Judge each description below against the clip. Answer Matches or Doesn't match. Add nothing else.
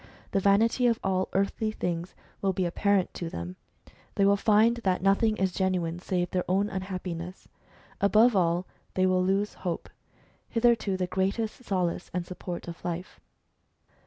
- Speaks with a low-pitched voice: Doesn't match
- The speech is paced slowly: Doesn't match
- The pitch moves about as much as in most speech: Doesn't match